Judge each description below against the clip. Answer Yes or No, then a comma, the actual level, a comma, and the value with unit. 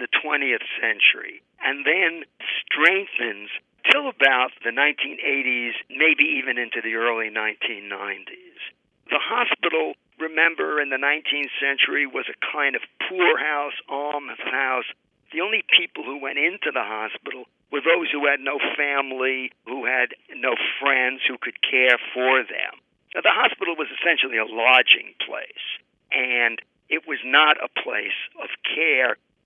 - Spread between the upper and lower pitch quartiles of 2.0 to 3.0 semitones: No, average, 3.9 semitones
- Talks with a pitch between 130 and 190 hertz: Yes, medium, 140 Hz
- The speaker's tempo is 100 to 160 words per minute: Yes, average, 140 wpm